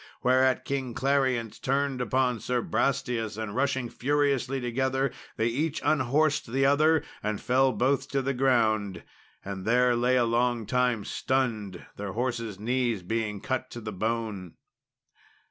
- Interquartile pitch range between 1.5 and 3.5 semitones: Yes, average, 3.0 semitones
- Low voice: Yes, low, 125 Hz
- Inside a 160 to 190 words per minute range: No, average, 145 wpm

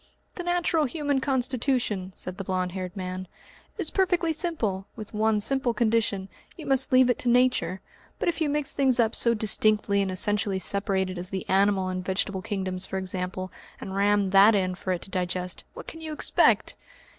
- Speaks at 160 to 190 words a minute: Yes, average, 185 wpm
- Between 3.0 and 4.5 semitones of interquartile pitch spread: No, wide, 5.4 semitones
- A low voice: No, high, 205 Hz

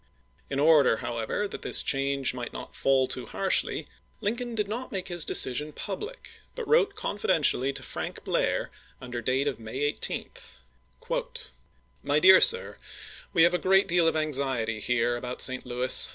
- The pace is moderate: Yes, average, 165 wpm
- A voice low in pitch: No, medium, 150 Hz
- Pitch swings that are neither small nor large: No, wide, 7.6 semitones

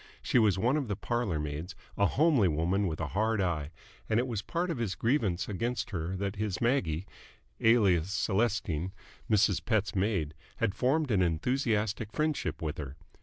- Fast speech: No, average, 170 wpm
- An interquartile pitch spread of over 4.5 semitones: Yes, average, 5.0 semitones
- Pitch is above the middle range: No, low, 100 Hz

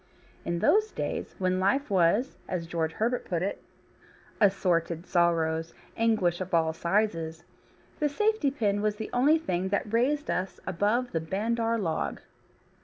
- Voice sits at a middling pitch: No, high, 195 Hz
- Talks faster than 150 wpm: No, average, 145 wpm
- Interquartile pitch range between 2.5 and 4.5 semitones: No, average, 5.3 semitones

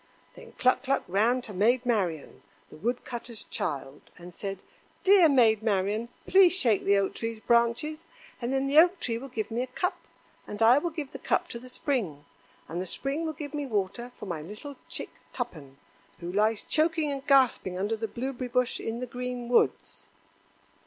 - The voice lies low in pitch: No, high, 235 Hz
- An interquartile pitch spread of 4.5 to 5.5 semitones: Yes, average, 5.2 semitones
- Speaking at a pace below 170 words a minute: No, average, 190 wpm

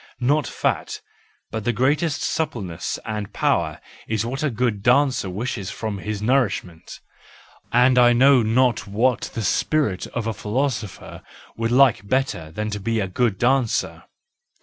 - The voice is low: Yes, low, 115 Hz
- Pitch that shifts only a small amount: No, average, 3.8 semitones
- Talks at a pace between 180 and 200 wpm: No, average, 145 wpm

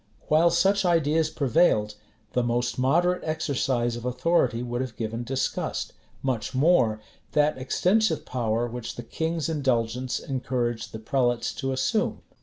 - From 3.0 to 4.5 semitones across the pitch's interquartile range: No, average, 5.0 semitones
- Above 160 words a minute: No, slow, 135 wpm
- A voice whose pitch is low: Yes, low, 130 Hz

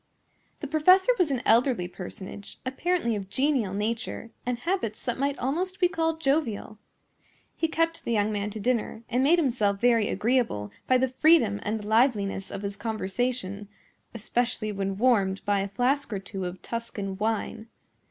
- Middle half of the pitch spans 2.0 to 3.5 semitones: No, average, 5.0 semitones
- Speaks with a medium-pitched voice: No, high, 230 Hz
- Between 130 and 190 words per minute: Yes, average, 160 wpm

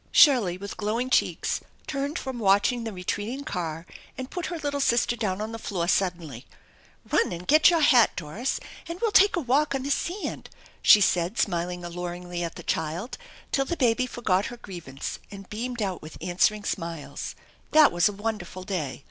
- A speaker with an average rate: Yes, average, 185 wpm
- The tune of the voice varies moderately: No, wide, 6.5 semitones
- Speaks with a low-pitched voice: No, high, 210 Hz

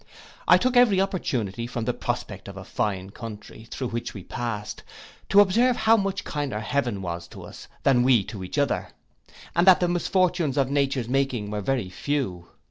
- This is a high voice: No, low, 130 Hz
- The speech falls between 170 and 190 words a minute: Yes, average, 185 wpm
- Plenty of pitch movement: Yes, wide, 8.8 semitones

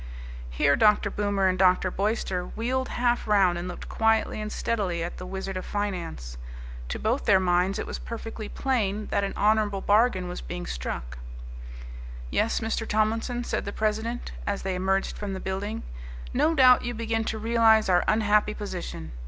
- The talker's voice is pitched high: Yes, high, 205 Hz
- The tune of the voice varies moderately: Yes, average, 3.2 semitones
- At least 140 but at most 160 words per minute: No, average, 170 wpm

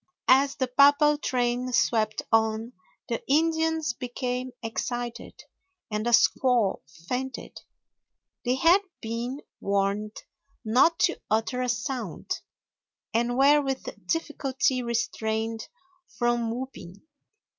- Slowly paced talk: Yes, slow, 100 wpm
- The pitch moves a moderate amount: Yes, average, 3.0 semitones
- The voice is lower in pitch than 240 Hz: No, high, 245 Hz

